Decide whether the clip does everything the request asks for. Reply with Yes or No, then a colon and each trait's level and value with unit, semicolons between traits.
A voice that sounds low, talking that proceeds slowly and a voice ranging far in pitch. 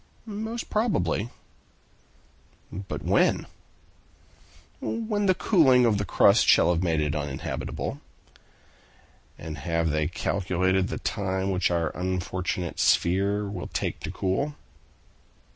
Yes: very low, 95 Hz; slow, 110 wpm; wide, 6.5 semitones